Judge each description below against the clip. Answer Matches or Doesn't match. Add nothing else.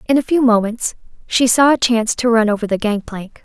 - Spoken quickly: Matches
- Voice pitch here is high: Matches